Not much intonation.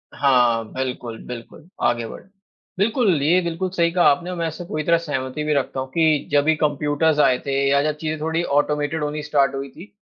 No: average, 3.2 semitones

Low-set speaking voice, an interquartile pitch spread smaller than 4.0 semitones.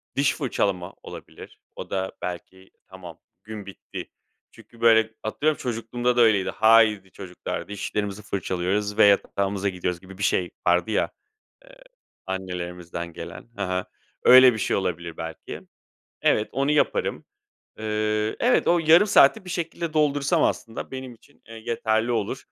No: low, 105 Hz; average, 4.5 semitones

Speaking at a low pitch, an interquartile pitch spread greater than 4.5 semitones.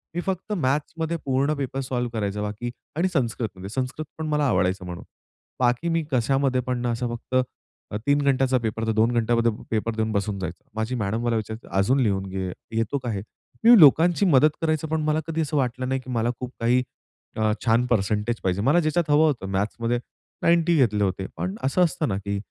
Yes: low, 125 Hz; average, 5.2 semitones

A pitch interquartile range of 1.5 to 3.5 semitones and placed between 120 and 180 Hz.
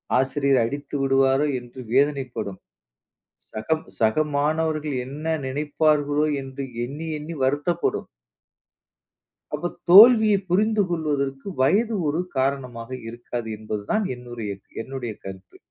No: average, 3.9 semitones; medium, 140 Hz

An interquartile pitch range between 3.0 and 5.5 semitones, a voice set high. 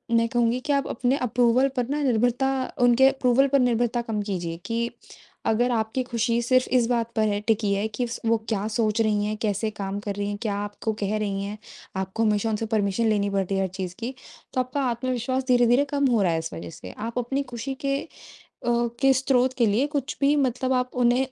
Yes: average, 3.3 semitones; high, 235 Hz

